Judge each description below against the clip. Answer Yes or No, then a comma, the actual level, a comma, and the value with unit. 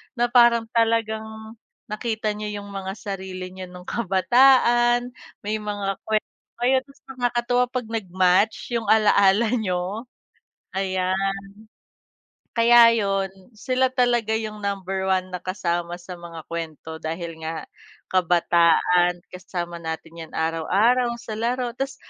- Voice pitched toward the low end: No, high, 200 Hz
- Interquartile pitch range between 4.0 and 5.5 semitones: Yes, average, 4.4 semitones